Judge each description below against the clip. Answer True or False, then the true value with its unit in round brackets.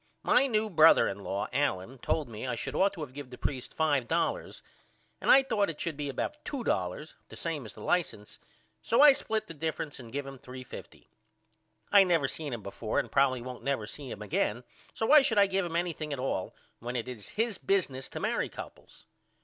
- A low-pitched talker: False (145 Hz)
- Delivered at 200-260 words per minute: True (205 wpm)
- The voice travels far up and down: True (7.2 semitones)